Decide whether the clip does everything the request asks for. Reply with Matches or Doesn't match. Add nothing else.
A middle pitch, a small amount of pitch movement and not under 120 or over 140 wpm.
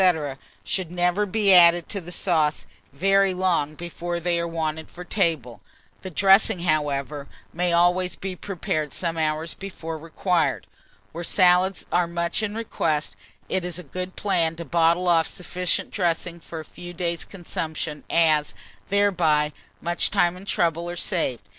Doesn't match